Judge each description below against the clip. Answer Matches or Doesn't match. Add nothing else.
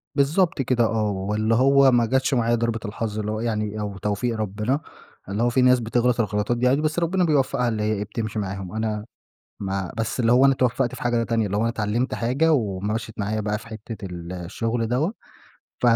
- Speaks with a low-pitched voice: Matches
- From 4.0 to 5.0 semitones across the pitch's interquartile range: Doesn't match